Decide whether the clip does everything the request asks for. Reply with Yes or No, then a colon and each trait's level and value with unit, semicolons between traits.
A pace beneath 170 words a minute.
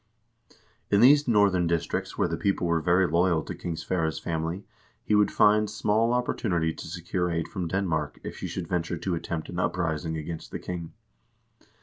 No: average, 185 wpm